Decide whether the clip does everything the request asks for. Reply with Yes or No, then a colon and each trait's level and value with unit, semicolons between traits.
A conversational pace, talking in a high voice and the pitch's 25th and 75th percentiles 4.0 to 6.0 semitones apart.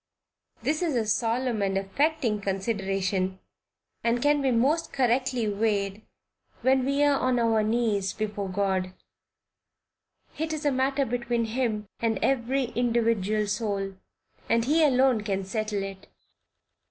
No: slow, 130 wpm; high, 230 Hz; average, 4.4 semitones